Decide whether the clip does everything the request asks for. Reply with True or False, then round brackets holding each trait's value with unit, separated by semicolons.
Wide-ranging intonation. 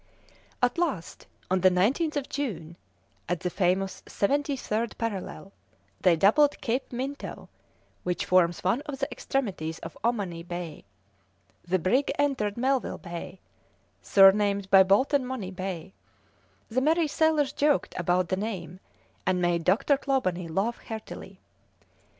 True (6.7 semitones)